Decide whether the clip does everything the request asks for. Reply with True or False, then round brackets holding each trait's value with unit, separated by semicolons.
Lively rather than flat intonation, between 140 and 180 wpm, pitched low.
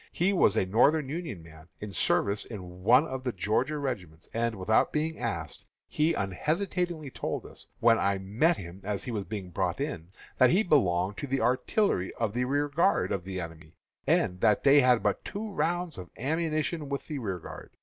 False (8.0 semitones; 190 wpm; 115 Hz)